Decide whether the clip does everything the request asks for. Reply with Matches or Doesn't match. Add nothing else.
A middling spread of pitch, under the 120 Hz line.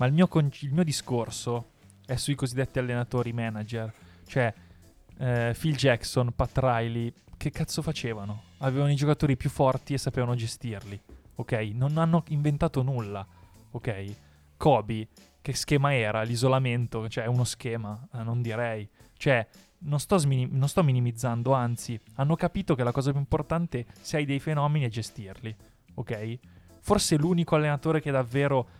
Doesn't match